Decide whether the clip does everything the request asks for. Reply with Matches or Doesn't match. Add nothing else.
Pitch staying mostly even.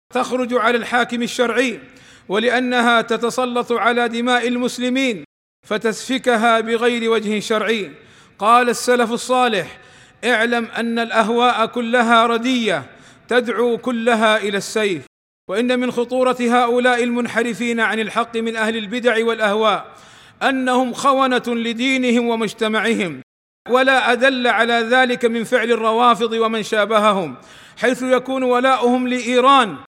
Matches